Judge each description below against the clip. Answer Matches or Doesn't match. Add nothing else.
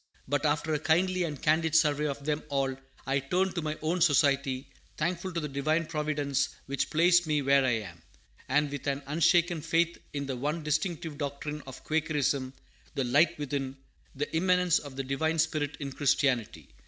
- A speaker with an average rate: Matches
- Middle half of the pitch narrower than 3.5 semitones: Matches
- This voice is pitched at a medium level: Matches